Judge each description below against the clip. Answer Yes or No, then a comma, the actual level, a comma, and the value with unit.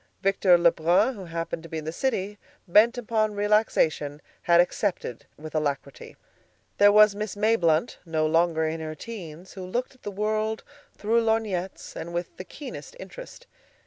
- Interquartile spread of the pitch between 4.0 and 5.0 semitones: Yes, average, 4.7 semitones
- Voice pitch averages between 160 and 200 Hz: Yes, high, 190 Hz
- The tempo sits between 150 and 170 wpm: Yes, average, 165 wpm